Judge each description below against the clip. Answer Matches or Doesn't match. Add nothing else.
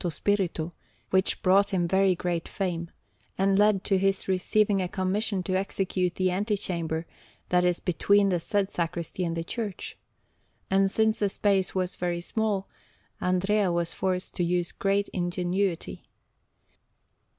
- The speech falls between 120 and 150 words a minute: Matches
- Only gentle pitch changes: Matches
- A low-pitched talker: Doesn't match